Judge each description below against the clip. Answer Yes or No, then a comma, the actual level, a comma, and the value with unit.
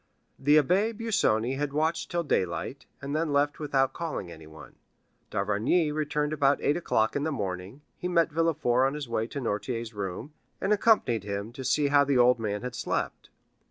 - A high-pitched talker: No, medium, 140 Hz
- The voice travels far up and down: Yes, wide, 5.7 semitones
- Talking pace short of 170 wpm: No, average, 180 wpm